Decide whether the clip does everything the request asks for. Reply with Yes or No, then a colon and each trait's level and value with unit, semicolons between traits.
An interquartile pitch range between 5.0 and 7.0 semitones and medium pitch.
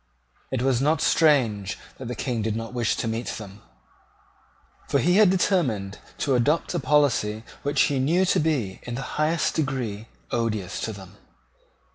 No: wide, 5.4 semitones; low, 125 Hz